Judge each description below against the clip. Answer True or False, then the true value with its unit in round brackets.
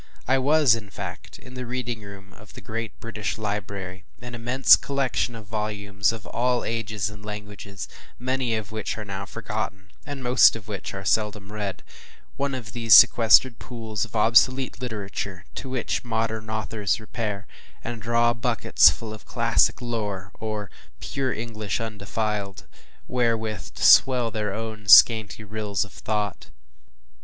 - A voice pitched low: True (110 Hz)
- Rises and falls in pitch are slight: True (2.3 semitones)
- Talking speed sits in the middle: True (150 wpm)